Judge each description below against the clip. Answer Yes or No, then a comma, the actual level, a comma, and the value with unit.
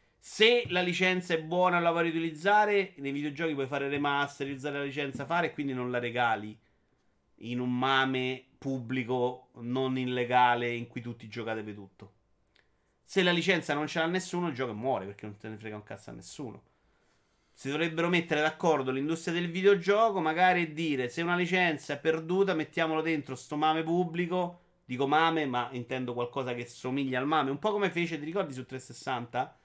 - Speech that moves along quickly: Yes, fast, 180 wpm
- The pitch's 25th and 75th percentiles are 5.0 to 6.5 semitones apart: Yes, wide, 5.5 semitones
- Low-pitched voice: No, medium, 145 Hz